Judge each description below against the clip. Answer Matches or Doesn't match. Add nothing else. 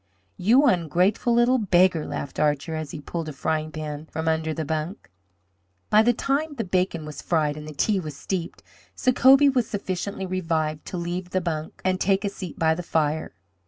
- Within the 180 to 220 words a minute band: Matches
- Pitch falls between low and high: Matches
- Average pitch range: Matches